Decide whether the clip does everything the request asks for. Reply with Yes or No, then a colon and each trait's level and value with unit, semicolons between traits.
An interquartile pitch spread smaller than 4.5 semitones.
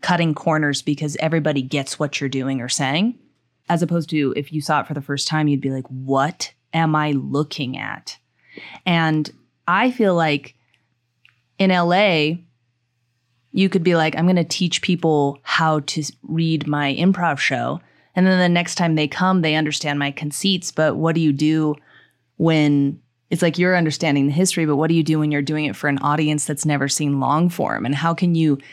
Yes: average, 2.9 semitones